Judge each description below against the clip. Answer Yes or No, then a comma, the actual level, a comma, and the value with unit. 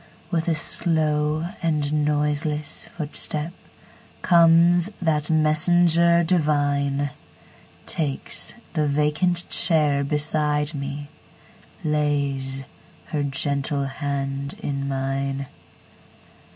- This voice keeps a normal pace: No, slow, 70 wpm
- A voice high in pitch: No, medium, 150 Hz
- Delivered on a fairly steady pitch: Yes, narrow, 2.3 semitones